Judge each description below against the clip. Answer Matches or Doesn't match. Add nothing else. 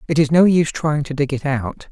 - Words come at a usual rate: Doesn't match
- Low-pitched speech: Doesn't match